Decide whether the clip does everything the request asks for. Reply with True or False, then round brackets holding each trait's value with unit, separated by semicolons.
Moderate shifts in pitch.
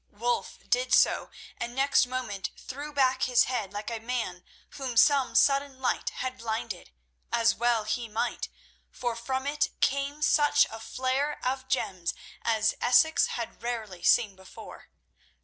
True (3.1 semitones)